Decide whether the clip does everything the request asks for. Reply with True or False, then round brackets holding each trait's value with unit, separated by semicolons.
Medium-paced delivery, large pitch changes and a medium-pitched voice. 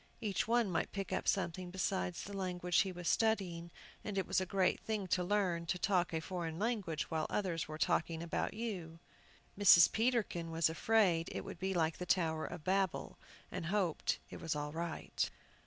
False (190 wpm; 3.0 semitones; 180 Hz)